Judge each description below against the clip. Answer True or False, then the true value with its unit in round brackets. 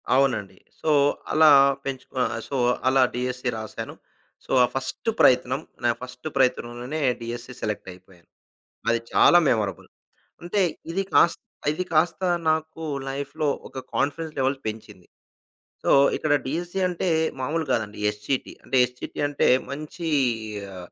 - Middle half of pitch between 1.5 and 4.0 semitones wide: False (4.9 semitones)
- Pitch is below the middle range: True (130 Hz)